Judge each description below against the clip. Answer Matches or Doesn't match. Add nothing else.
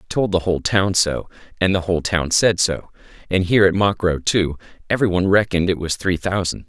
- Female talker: Doesn't match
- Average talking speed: Doesn't match